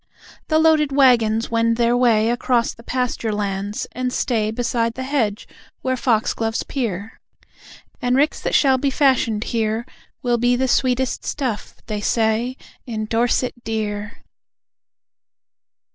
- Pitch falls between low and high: No, high, 235 Hz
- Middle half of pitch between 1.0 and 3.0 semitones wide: Yes, narrow, 2.6 semitones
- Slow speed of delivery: Yes, slow, 130 wpm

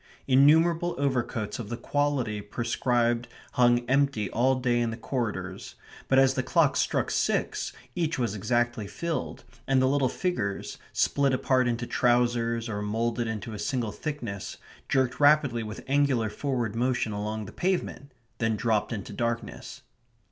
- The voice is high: No, low, 120 Hz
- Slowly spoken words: No, average, 150 wpm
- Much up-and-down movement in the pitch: No, average, 3.2 semitones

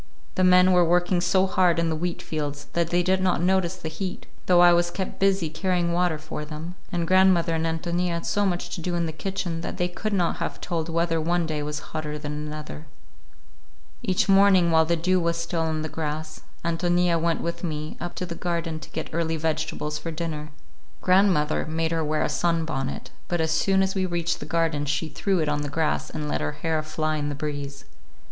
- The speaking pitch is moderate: Yes, medium, 165 Hz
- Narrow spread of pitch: Yes, narrow, 2.3 semitones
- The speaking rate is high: Yes, fast, 210 wpm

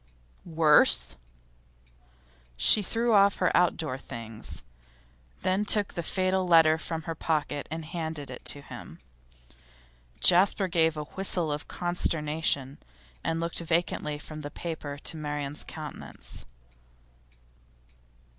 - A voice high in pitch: No, medium, 160 Hz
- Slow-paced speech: Yes, slow, 115 wpm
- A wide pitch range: No, average, 2.9 semitones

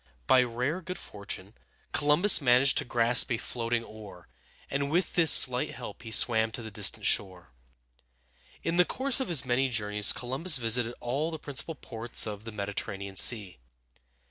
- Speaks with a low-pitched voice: Yes, low, 120 Hz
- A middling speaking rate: Yes, average, 165 wpm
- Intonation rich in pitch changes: No, average, 4.9 semitones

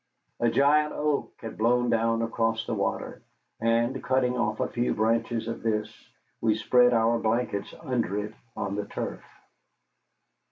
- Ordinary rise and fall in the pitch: No, narrow, 1.8 semitones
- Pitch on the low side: Yes, low, 115 Hz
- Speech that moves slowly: No, average, 150 wpm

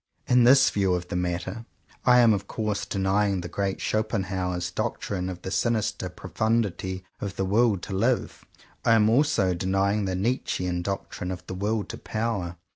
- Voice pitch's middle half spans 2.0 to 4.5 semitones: Yes, average, 3.3 semitones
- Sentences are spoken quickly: No, average, 170 wpm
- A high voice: No, low, 100 Hz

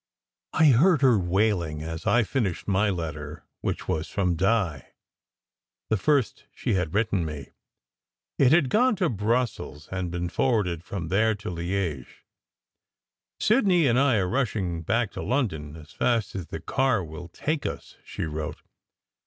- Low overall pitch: Yes, low, 100 Hz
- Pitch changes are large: Yes, wide, 6.8 semitones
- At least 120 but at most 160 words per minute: Yes, average, 155 wpm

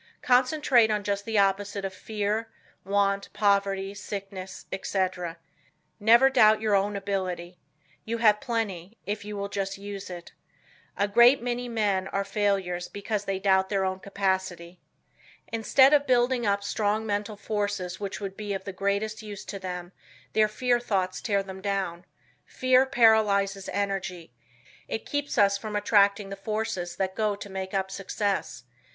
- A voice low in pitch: No, high, 200 Hz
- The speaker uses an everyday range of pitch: No, narrow, 2.0 semitones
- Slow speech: No, average, 155 wpm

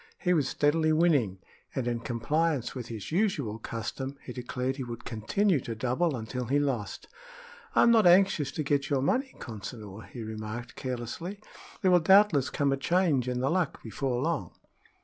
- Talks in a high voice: No, low, 135 Hz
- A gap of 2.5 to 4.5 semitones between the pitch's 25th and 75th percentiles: No, wide, 5.6 semitones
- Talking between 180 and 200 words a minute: No, average, 170 wpm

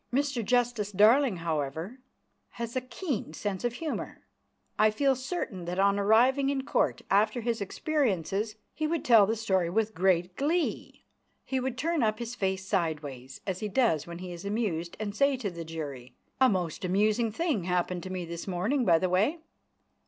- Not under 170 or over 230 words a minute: Yes, average, 180 wpm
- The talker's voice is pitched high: Yes, high, 210 Hz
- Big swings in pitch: Yes, wide, 5.8 semitones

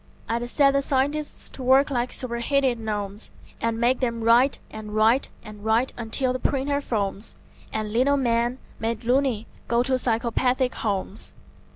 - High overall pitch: Yes, high, 240 Hz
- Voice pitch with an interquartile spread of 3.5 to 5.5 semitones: No, average, 2.8 semitones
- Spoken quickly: No, average, 155 wpm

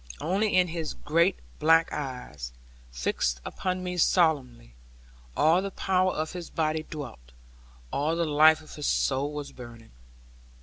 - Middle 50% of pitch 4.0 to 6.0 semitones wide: Yes, average, 4.5 semitones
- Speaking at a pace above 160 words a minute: No, average, 140 wpm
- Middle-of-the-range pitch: Yes, medium, 155 Hz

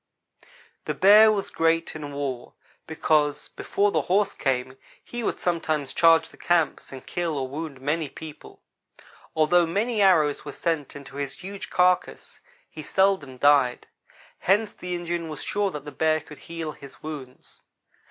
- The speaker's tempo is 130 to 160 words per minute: Yes, average, 155 wpm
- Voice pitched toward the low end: No, medium, 160 Hz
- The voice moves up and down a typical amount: Yes, average, 3.9 semitones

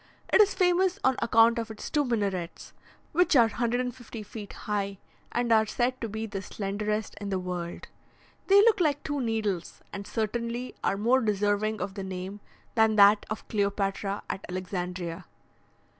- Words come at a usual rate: Yes, average, 160 wpm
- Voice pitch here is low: No, high, 215 Hz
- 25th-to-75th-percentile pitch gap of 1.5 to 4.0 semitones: Yes, average, 3.4 semitones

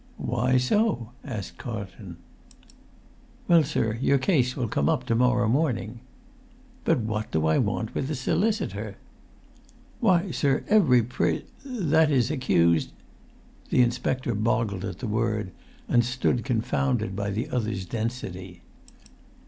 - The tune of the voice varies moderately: Yes, average, 4.1 semitones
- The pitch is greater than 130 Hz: No, low, 120 Hz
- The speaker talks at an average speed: No, slow, 125 wpm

